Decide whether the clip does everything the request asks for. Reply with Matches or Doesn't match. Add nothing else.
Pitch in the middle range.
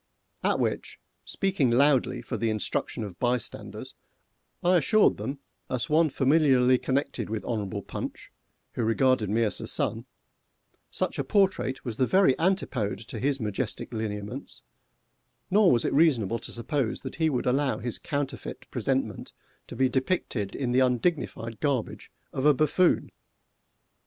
Doesn't match